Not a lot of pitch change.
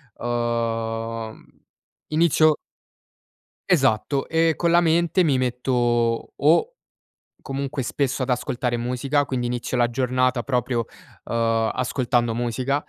No: average, 3.1 semitones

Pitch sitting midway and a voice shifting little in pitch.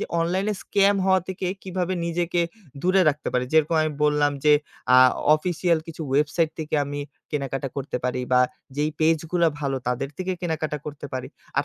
No: medium, 155 Hz; average, 3.5 semitones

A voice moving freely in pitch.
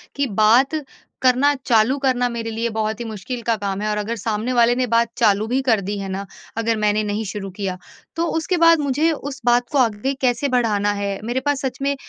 No: average, 3.8 semitones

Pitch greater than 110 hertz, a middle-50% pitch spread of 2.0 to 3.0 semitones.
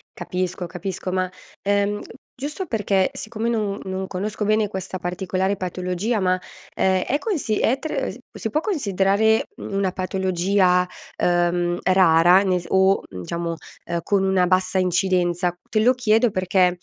Yes: high, 190 Hz; narrow, 2.4 semitones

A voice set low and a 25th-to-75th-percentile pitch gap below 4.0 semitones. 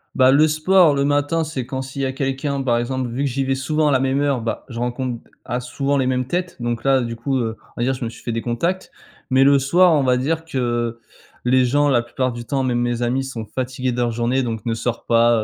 Yes: low, 130 Hz; average, 2.7 semitones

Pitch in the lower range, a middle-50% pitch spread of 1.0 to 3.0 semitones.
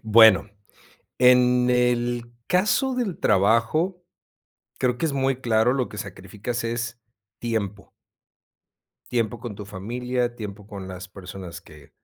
No: low, 120 Hz; average, 3.4 semitones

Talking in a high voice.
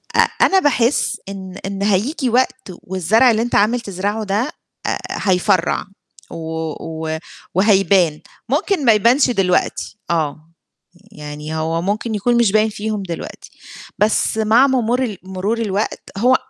Yes: high, 205 Hz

